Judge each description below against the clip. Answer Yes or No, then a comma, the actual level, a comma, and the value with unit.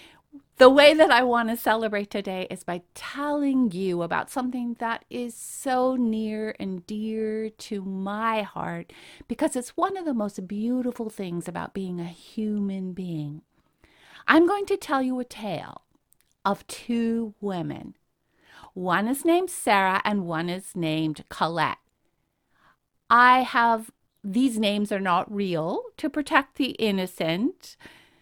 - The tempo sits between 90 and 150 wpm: Yes, average, 140 wpm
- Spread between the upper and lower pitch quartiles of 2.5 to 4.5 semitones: No, average, 4.9 semitones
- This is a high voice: Yes, high, 220 Hz